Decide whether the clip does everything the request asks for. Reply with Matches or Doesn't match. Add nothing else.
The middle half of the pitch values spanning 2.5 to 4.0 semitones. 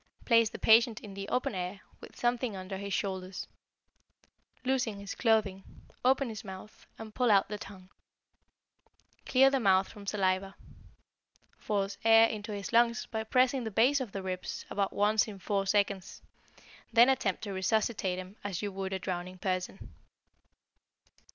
Matches